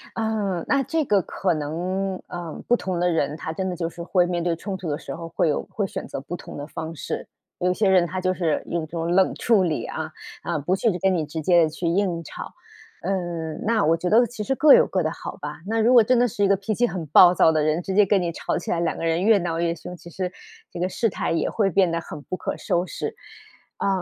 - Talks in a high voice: No, medium, 180 Hz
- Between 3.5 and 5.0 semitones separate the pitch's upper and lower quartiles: No, average, 2.9 semitones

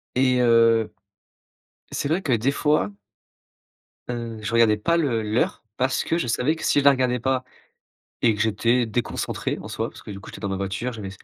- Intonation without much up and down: No, average, 3.2 semitones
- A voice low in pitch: Yes, low, 120 Hz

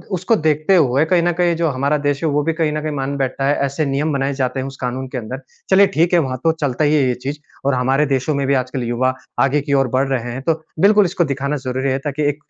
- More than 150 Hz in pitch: No, medium, 140 Hz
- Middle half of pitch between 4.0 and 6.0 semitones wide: No, average, 2.9 semitones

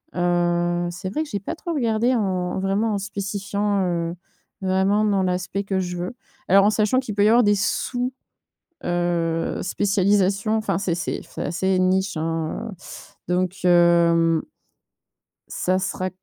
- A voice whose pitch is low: No, high, 190 Hz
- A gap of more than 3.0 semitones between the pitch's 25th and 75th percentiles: No, average, 2.7 semitones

